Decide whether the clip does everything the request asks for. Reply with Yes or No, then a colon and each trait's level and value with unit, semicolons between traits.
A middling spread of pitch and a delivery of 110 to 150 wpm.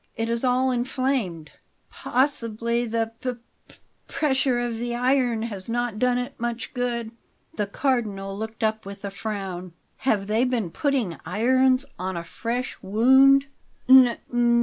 Yes: average, 3.2 semitones; average, 140 wpm